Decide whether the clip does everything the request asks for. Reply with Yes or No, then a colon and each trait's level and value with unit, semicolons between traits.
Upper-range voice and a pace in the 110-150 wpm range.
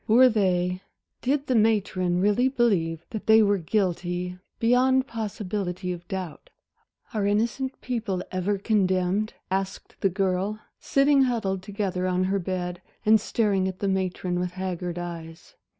Yes: high, 195 Hz; average, 140 wpm